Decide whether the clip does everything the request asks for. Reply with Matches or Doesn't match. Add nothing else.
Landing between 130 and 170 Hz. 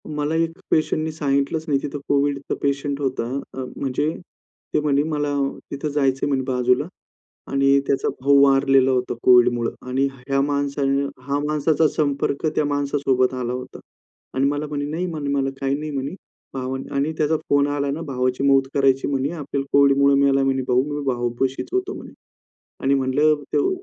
Matches